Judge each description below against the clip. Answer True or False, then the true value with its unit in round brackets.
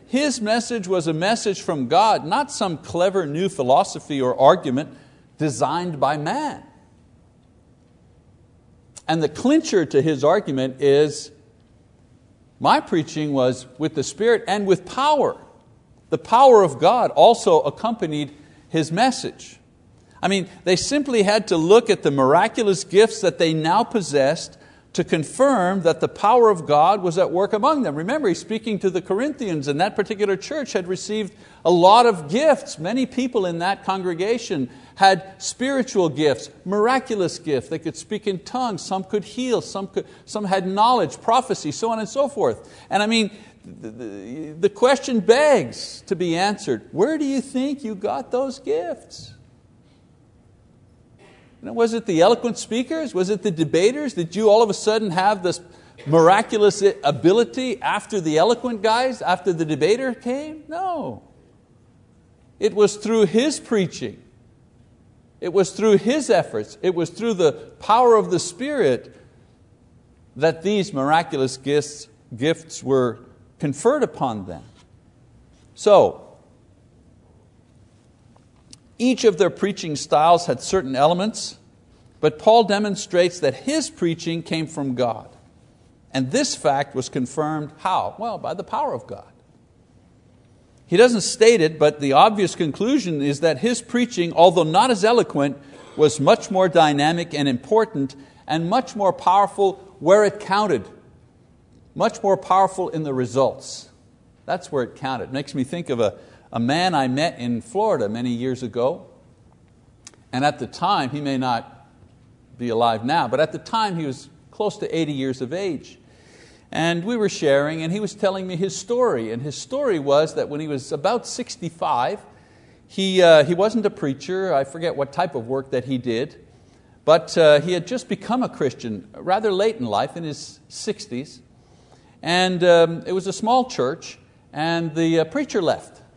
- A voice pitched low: False (180 Hz)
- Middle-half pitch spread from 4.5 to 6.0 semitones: False (7.0 semitones)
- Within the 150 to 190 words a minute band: True (160 wpm)